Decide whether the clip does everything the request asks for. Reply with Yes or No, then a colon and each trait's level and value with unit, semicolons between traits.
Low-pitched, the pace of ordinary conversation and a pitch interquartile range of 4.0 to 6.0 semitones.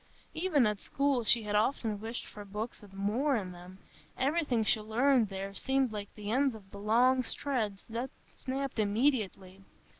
No: high, 220 Hz; average, 160 wpm; average, 4.4 semitones